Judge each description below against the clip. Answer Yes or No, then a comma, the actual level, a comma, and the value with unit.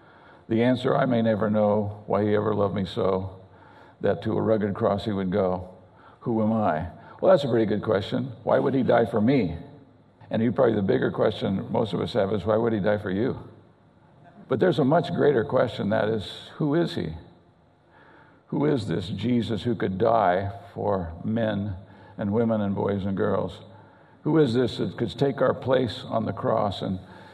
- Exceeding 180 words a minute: Yes, average, 200 wpm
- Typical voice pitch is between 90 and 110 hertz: Yes, low, 105 Hz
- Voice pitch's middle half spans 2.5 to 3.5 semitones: Yes, average, 3.0 semitones